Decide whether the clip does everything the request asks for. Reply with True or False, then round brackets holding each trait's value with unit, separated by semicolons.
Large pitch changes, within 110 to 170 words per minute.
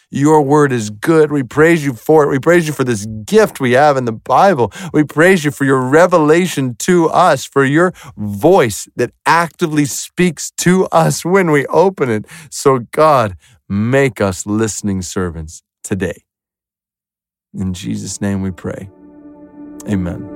True (7.4 semitones; 155 wpm)